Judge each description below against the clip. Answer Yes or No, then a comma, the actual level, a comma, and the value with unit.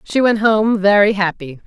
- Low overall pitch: No, high, 205 Hz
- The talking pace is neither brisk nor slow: Yes, average, 180 wpm